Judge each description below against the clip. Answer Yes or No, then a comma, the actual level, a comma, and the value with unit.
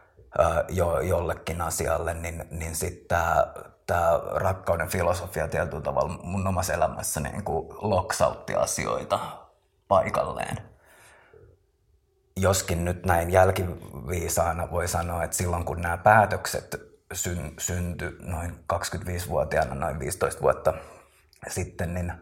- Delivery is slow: No, average, 105 wpm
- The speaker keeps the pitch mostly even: Yes, narrow, 1.4 semitones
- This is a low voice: Yes, very low, 85 Hz